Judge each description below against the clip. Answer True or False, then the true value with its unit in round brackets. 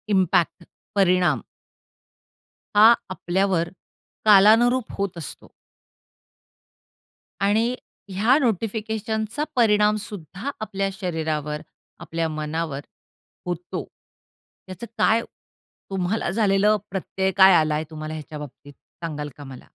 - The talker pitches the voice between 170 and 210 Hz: True (185 Hz)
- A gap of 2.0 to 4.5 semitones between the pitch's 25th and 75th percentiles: False (4.9 semitones)